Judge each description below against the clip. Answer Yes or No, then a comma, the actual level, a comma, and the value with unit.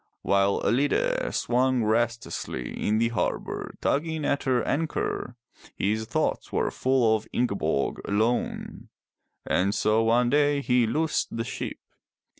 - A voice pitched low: Yes, low, 120 Hz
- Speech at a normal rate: No, slow, 125 wpm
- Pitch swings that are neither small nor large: Yes, average, 3.3 semitones